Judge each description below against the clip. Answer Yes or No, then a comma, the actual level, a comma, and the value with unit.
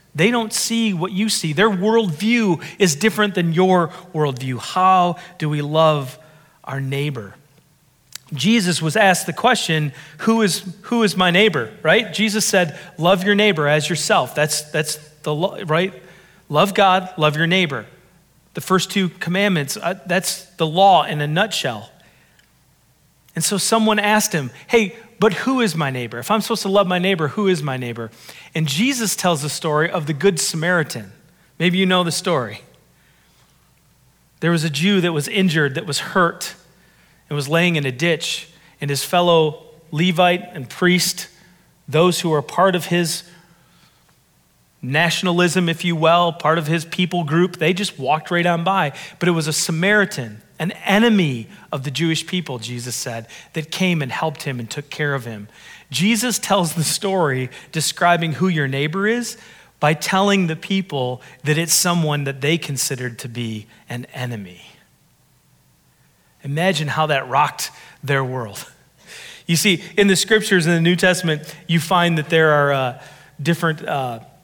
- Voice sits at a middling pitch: Yes, medium, 170 Hz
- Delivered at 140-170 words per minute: Yes, average, 165 wpm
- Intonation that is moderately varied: Yes, average, 3.8 semitones